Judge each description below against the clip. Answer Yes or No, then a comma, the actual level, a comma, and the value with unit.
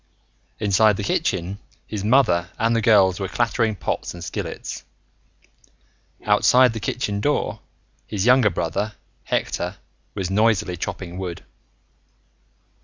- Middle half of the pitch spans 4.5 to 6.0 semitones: No, average, 3.2 semitones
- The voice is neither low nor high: No, low, 105 Hz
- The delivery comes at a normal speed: No, slow, 115 wpm